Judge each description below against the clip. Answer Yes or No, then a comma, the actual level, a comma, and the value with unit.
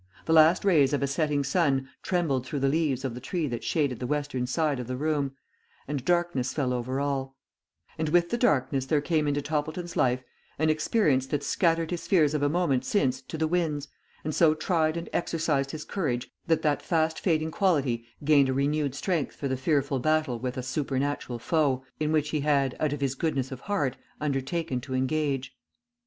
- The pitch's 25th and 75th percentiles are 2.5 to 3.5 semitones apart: Yes, average, 3.1 semitones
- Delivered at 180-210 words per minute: Yes, average, 200 wpm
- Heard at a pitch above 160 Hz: No, medium, 145 Hz